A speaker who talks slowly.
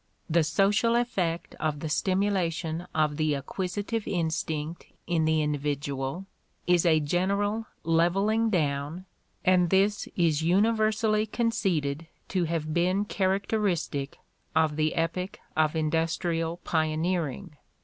Yes: slow, 110 wpm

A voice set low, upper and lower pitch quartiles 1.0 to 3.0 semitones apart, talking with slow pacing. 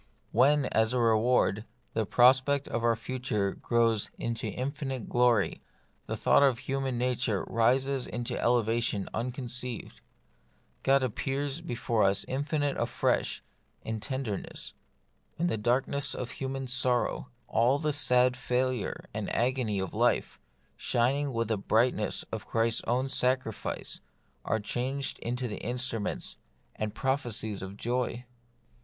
Yes: low, 125 Hz; narrow, 2.6 semitones; slow, 130 wpm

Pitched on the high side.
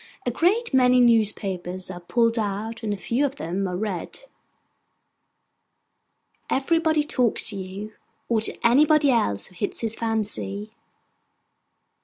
Yes: high, 225 Hz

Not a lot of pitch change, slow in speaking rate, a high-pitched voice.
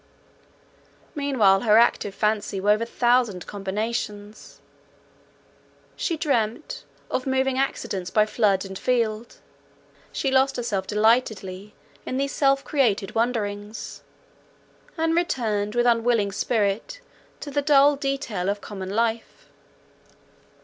No: average, 4.4 semitones; slow, 110 wpm; high, 225 Hz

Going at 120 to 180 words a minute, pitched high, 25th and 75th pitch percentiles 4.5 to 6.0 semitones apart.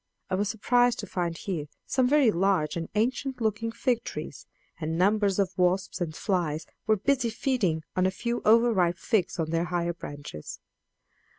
Yes: average, 175 wpm; high, 195 Hz; average, 5.2 semitones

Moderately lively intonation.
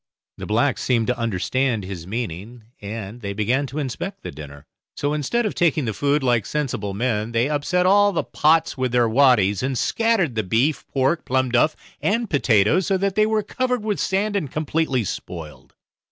No: wide, 7.4 semitones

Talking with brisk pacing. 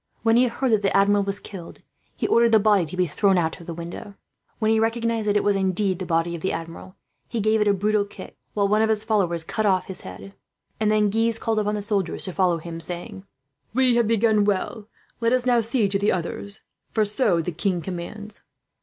Yes: fast, 235 wpm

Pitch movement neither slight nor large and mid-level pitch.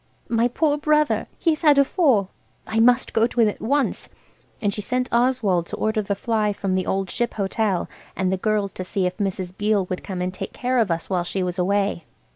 No: average, 4.5 semitones; high, 210 Hz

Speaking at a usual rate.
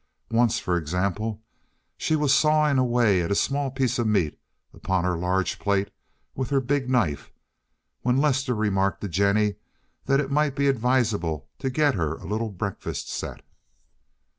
Yes: average, 160 wpm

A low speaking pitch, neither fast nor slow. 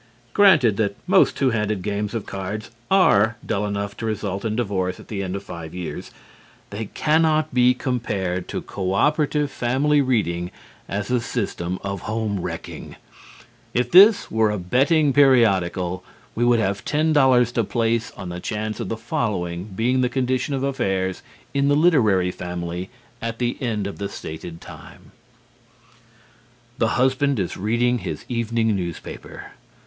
Yes: low, 110 Hz; average, 155 wpm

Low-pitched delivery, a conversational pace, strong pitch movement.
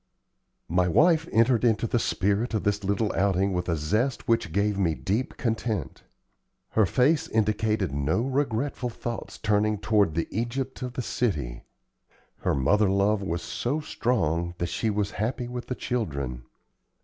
No: low, 105 Hz; average, 155 wpm; average, 4.6 semitones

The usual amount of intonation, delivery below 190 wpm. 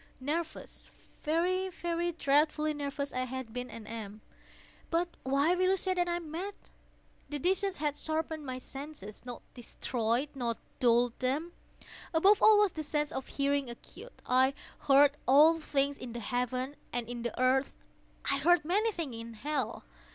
Yes: average, 4.7 semitones; average, 155 wpm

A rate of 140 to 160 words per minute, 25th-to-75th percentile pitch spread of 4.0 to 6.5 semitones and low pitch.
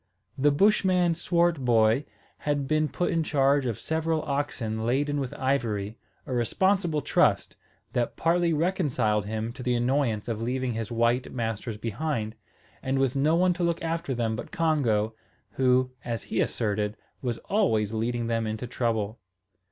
Yes: average, 150 wpm; wide, 5.4 semitones; low, 130 Hz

